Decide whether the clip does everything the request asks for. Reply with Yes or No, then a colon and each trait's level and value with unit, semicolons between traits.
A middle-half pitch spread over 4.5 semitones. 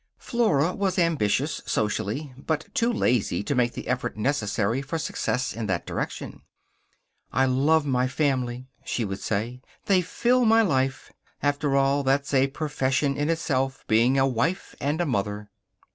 No: average, 4.2 semitones